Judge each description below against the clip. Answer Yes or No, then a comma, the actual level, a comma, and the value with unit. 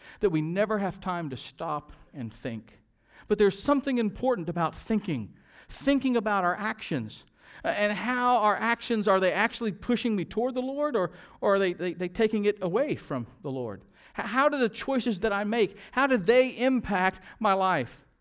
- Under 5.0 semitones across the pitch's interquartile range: No, wide, 5.5 semitones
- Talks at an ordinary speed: Yes, average, 185 wpm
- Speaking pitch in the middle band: No, high, 205 Hz